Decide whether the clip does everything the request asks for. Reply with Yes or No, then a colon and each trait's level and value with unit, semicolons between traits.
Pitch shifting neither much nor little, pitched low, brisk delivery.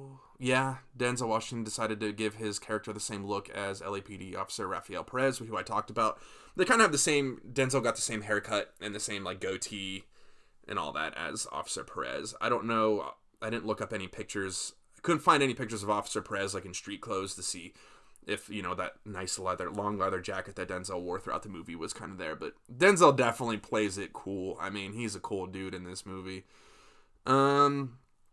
Yes: average, 3.6 semitones; low, 105 Hz; fast, 210 wpm